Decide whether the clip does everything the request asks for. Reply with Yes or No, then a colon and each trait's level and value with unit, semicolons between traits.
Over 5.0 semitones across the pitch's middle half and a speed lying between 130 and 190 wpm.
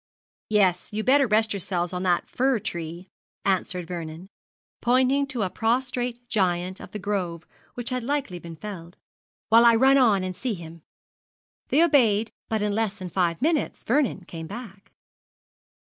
Yes: wide, 5.4 semitones; average, 160 wpm